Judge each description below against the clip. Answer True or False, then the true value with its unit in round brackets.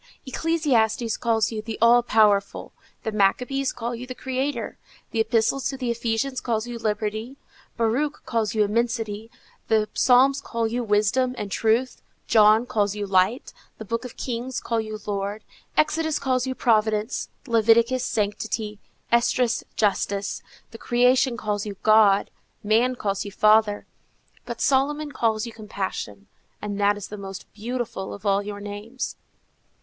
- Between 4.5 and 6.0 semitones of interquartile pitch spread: False (3.0 semitones)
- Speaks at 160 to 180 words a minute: False (150 wpm)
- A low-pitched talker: False (225 Hz)